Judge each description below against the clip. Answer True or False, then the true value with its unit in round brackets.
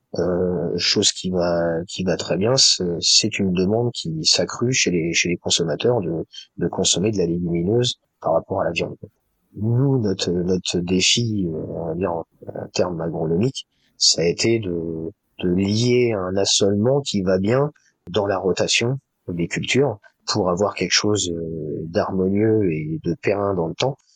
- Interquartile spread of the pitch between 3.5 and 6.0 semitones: True (4.2 semitones)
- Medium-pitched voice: False (95 Hz)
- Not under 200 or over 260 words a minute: False (165 wpm)